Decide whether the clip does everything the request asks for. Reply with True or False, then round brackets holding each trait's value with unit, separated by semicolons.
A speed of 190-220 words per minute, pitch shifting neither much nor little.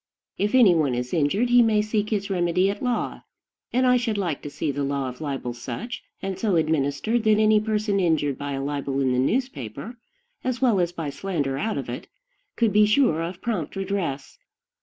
False (200 wpm; 7.2 semitones)